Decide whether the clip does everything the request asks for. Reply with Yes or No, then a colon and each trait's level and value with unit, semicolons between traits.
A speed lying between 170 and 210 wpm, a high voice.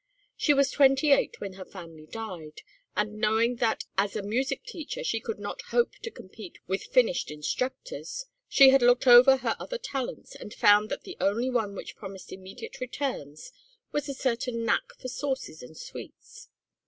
Yes: average, 175 wpm; high, 235 Hz